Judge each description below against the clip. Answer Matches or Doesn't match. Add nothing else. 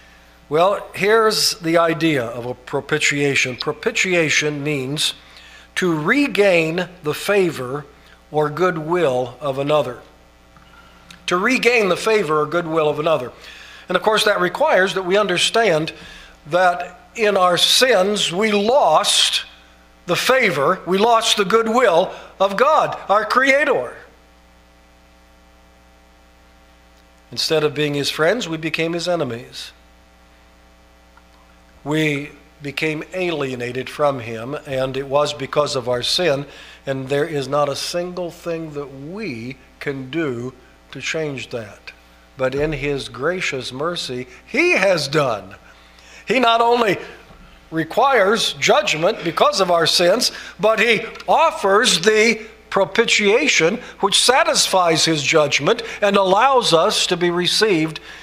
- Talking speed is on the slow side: Matches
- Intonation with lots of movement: Matches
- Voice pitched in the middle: Matches